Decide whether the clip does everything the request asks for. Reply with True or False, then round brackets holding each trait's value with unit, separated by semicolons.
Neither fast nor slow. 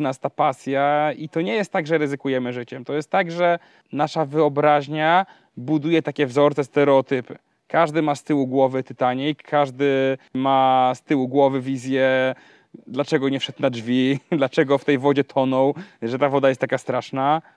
False (165 wpm)